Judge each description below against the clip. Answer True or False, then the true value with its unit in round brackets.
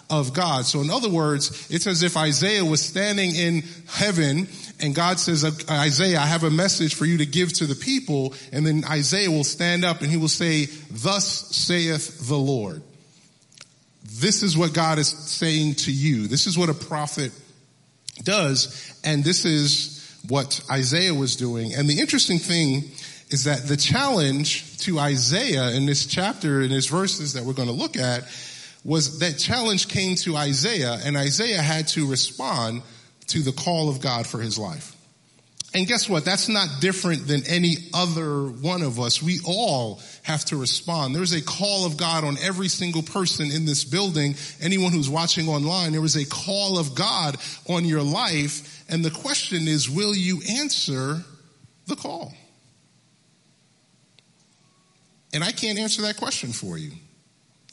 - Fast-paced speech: False (170 wpm)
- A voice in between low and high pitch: True (155 Hz)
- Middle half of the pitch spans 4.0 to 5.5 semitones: False (3.6 semitones)